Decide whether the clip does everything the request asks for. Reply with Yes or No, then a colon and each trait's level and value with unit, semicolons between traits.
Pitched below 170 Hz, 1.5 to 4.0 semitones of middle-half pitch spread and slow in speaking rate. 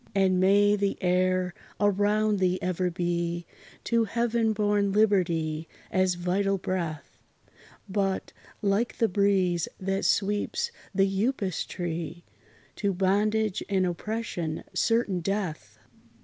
No: high, 195 Hz; narrow, 2.6 semitones; slow, 110 wpm